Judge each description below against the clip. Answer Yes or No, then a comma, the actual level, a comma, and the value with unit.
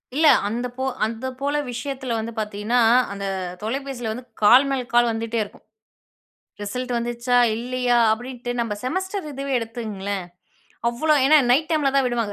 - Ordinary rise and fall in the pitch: Yes, average, 3.1 semitones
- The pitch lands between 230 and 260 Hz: Yes, high, 245 Hz